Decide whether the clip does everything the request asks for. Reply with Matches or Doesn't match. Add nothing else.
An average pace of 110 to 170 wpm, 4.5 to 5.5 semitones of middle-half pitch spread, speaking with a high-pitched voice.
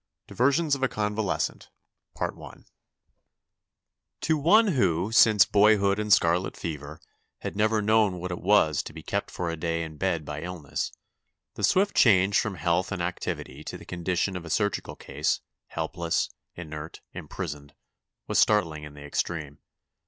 Doesn't match